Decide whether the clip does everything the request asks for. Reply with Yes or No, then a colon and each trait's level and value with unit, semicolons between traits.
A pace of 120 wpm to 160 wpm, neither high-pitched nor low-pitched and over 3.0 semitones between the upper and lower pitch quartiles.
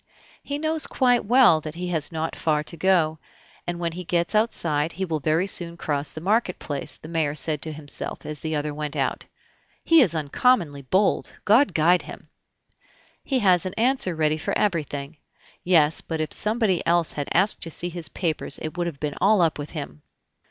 No: average, 195 wpm; medium, 165 Hz; average, 3.6 semitones